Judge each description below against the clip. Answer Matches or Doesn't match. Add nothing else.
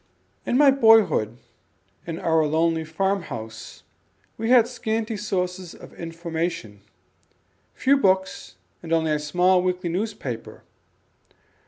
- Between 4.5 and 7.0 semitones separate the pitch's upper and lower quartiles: Matches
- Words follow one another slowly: Matches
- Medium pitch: Matches